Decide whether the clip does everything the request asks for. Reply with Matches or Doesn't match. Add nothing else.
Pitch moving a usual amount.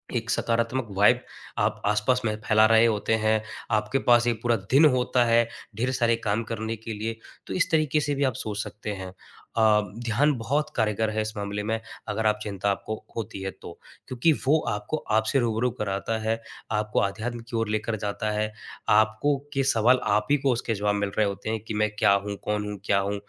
Doesn't match